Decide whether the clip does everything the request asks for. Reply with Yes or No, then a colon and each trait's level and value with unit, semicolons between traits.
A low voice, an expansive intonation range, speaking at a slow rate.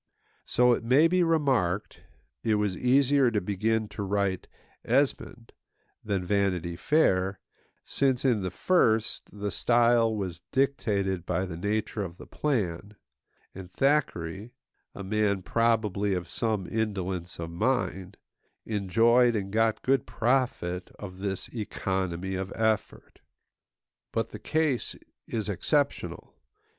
No: low, 105 Hz; average, 4.1 semitones; slow, 125 wpm